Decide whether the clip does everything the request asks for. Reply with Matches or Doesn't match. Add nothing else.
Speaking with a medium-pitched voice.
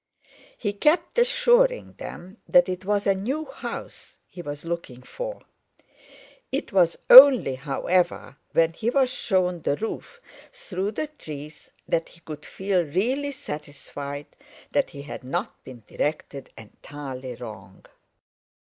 Matches